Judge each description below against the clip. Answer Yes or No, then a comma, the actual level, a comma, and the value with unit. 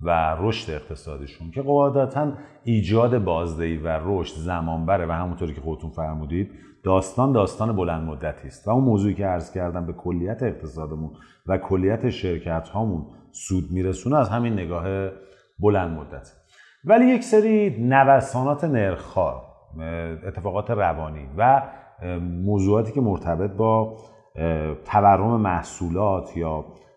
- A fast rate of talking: No, average, 120 wpm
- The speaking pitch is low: Yes, very low, 95 Hz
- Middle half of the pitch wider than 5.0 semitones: Yes, wide, 5.4 semitones